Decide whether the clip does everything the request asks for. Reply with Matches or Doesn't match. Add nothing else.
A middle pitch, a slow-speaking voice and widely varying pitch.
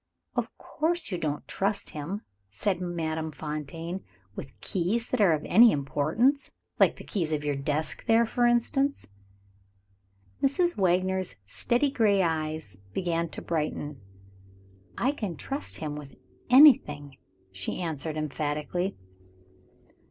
Matches